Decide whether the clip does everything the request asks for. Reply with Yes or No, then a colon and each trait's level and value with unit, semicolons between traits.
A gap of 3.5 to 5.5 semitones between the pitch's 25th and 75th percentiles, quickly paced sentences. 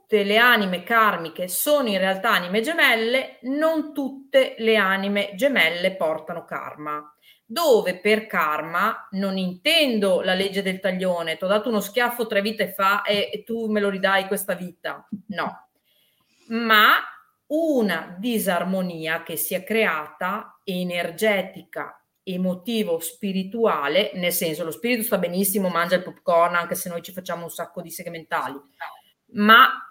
No: average, 4.2 semitones; average, 140 wpm